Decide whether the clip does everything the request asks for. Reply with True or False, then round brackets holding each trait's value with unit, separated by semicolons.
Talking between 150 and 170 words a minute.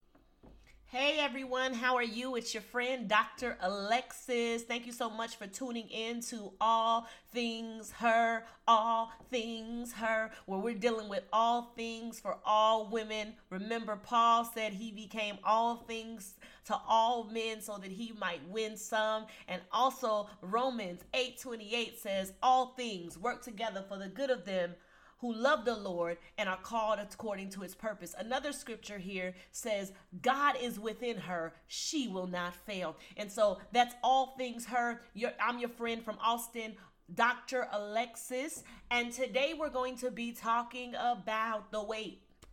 True (155 wpm)